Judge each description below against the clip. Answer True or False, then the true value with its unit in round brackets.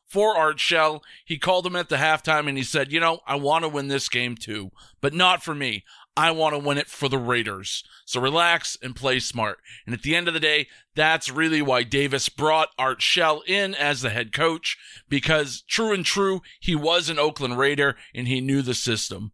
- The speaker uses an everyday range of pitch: True (4.0 semitones)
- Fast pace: True (220 wpm)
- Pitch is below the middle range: False (145 Hz)